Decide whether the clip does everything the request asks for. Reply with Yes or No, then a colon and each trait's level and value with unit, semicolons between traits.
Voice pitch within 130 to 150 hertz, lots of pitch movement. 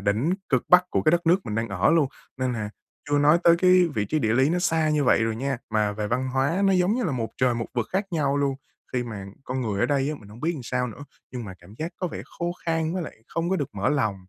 Yes: low, 135 Hz; wide, 6.6 semitones